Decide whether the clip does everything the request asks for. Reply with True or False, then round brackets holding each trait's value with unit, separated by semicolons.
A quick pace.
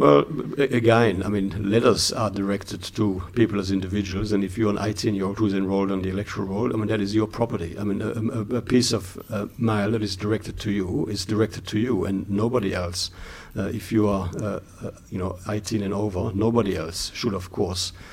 True (210 wpm)